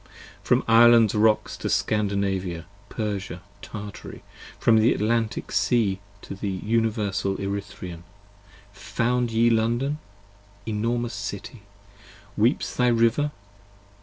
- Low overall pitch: Yes, low, 110 Hz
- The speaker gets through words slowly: Yes, slow, 105 wpm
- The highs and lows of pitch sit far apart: No, average, 2.7 semitones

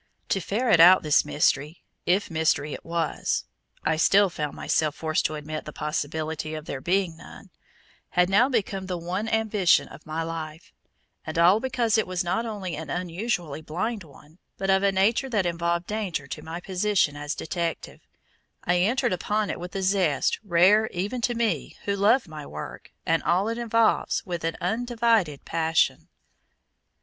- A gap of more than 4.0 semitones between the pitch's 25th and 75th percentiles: Yes, average, 4.4 semitones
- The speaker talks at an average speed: Yes, average, 170 wpm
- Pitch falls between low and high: Yes, medium, 180 Hz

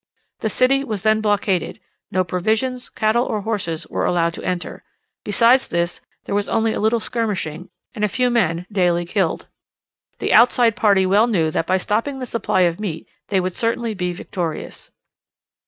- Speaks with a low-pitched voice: No, high, 205 Hz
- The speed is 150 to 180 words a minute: Yes, average, 170 wpm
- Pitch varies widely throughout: No, average, 4.2 semitones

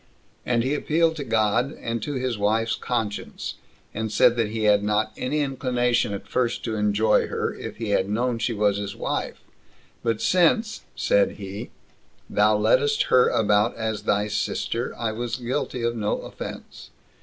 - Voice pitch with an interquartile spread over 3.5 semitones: No, average, 3.1 semitones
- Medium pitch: No, low, 115 Hz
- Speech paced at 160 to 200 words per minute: Yes, average, 165 wpm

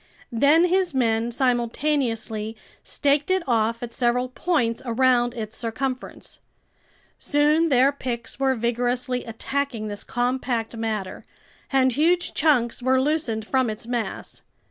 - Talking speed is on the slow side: Yes, slow, 120 wpm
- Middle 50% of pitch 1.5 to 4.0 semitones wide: Yes, average, 3.4 semitones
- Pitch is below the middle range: No, very high, 250 Hz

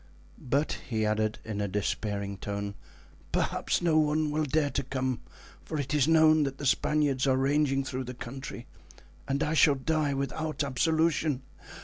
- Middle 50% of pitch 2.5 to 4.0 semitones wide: Yes, average, 3.5 semitones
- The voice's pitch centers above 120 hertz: Yes, medium, 140 Hz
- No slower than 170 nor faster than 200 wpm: No, average, 160 wpm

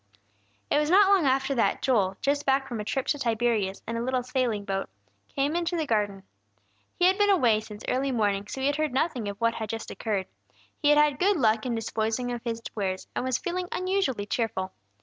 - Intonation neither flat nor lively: Yes, average, 5.0 semitones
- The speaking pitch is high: Yes, high, 245 Hz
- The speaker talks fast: Yes, fast, 215 wpm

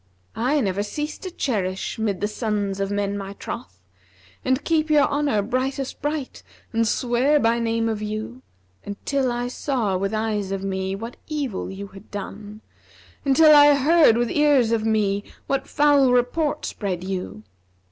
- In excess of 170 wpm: No, average, 165 wpm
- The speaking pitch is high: Yes, high, 225 Hz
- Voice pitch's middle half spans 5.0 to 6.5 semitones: Yes, wide, 5.4 semitones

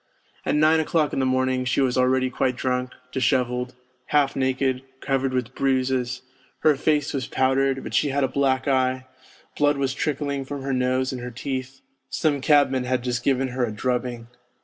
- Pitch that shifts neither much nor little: No, narrow, 1.4 semitones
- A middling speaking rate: Yes, average, 180 wpm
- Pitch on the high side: No, low, 130 Hz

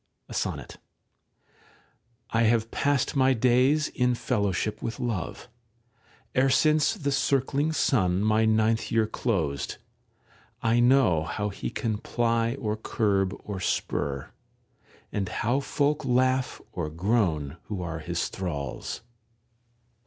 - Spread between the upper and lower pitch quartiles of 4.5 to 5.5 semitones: Yes, average, 5.2 semitones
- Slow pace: Yes, slow, 115 wpm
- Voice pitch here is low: Yes, low, 115 Hz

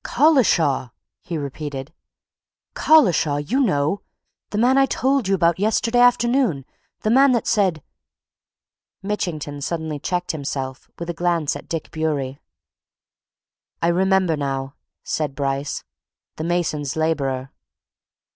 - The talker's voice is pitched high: No, medium, 165 Hz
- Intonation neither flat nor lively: No, wide, 6.4 semitones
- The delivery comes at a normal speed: No, slow, 120 wpm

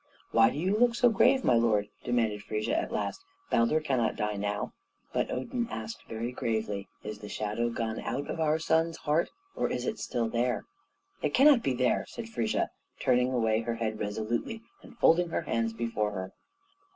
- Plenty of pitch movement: Yes, wide, 6.7 semitones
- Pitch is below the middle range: Yes, low, 120 Hz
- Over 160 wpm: Yes, average, 185 wpm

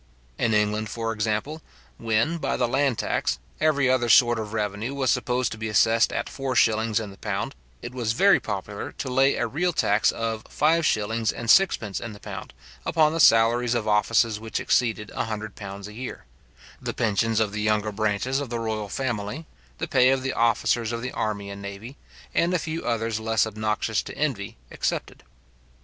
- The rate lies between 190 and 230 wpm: Yes, average, 195 wpm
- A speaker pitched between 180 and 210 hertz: No, low, 115 Hz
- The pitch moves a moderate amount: Yes, average, 3.1 semitones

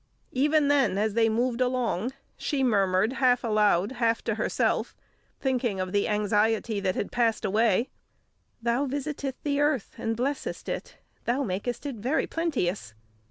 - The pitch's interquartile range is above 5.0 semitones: No, average, 4.3 semitones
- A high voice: Yes, high, 235 Hz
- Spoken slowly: No, average, 150 wpm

